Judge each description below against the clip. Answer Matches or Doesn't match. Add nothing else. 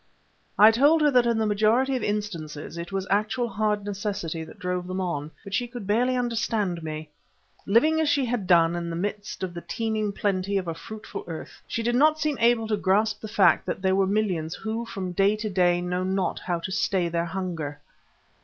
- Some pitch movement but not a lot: Matches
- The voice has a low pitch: Doesn't match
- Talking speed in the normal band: Doesn't match